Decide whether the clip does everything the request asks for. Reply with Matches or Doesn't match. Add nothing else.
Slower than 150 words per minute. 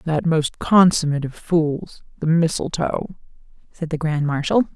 Matches